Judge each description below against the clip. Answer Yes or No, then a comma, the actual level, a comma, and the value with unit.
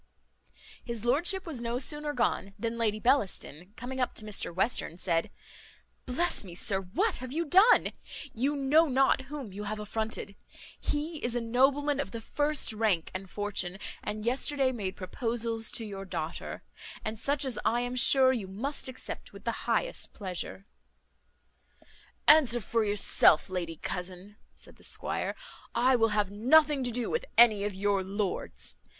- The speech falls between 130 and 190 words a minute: Yes, average, 160 wpm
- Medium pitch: No, high, 230 Hz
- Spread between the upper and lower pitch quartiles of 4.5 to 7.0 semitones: Yes, average, 4.9 semitones